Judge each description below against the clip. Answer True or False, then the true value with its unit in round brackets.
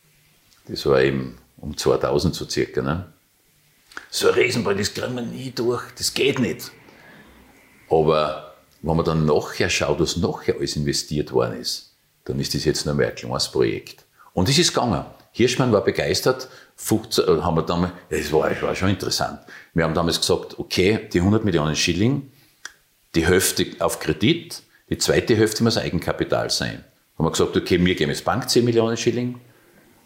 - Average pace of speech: True (175 wpm)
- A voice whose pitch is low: True (90 Hz)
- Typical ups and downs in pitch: False (7.5 semitones)